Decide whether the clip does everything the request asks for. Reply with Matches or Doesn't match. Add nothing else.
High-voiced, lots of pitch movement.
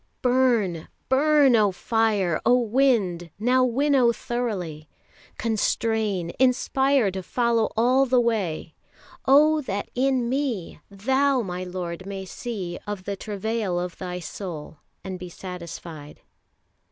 Matches